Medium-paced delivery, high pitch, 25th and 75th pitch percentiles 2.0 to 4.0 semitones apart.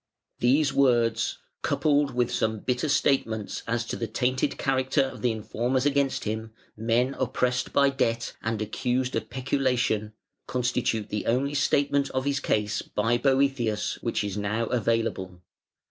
No: average, 145 wpm; low, 125 Hz; average, 3.3 semitones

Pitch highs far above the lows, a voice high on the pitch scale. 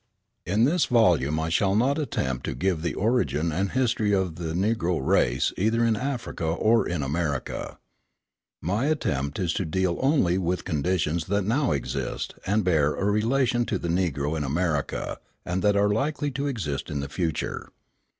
No: wide, 6.2 semitones; very low, 95 Hz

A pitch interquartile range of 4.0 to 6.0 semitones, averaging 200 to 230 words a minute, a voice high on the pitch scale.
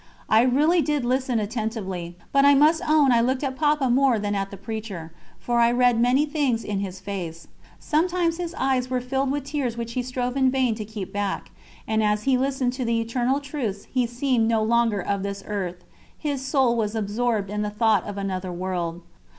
Yes: average, 4.5 semitones; fast, 205 wpm; high, 235 Hz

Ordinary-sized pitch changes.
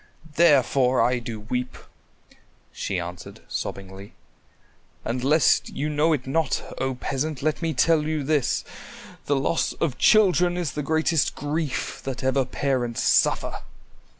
Yes: average, 3.8 semitones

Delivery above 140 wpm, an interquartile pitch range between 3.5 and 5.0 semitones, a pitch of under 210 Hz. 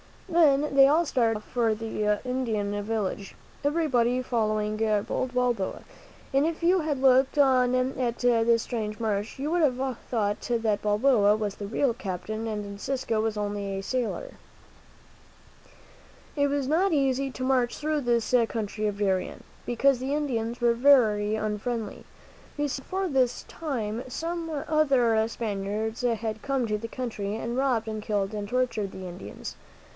No: average, 150 wpm; average, 4.1 semitones; high, 235 Hz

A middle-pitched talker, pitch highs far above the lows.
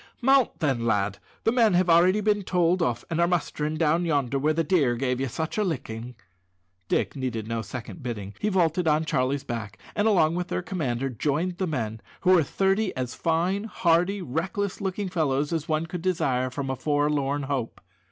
Yes: medium, 155 Hz; wide, 5.8 semitones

